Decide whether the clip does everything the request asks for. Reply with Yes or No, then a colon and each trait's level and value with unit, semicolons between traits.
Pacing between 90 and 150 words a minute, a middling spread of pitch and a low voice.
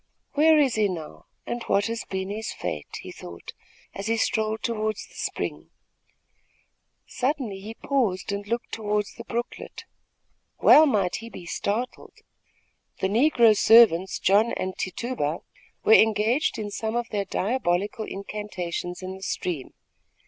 No: average, 140 wpm; average, 3.5 semitones; high, 215 Hz